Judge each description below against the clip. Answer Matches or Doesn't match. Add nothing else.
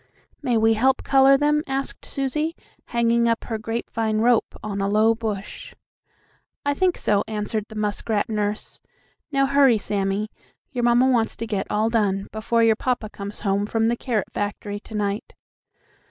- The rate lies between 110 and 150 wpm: Doesn't match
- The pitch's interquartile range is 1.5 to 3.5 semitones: Matches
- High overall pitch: Matches